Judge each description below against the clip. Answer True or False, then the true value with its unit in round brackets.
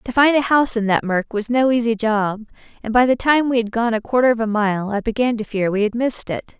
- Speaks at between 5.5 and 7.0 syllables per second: True (5.9 syllables/s)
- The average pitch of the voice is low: False (230 Hz)